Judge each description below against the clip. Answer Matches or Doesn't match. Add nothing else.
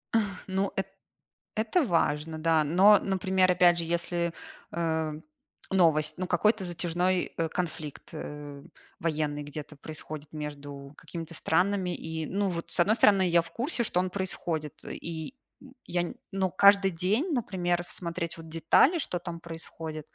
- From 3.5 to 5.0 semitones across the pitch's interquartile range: Doesn't match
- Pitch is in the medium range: Matches